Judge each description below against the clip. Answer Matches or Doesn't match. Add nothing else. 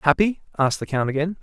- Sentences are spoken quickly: Matches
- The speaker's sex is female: Doesn't match